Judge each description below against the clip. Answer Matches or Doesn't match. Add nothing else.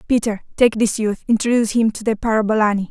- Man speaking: Doesn't match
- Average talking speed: Matches